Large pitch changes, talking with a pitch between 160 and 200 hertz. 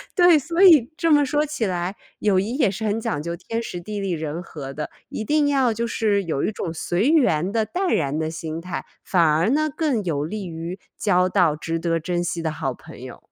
Yes: wide, 6.8 semitones; high, 190 Hz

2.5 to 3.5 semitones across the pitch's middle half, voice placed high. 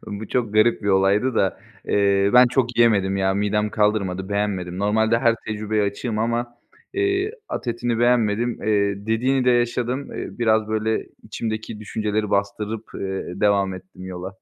No: average, 2.8 semitones; low, 110 Hz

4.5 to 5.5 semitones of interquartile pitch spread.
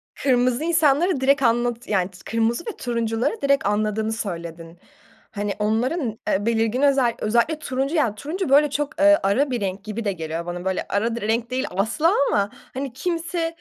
Yes: average, 5.2 semitones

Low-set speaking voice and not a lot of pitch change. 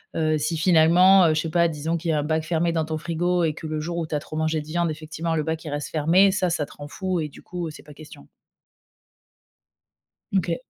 No: medium, 160 Hz; narrow, 1.8 semitones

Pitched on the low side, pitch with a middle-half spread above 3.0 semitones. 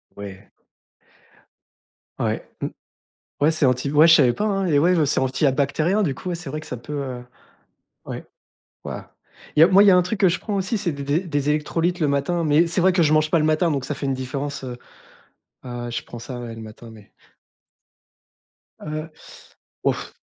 No: medium, 150 Hz; average, 4.6 semitones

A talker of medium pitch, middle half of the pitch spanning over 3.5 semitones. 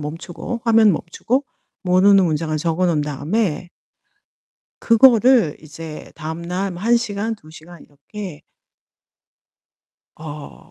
Yes: medium, 175 Hz; average, 5.3 semitones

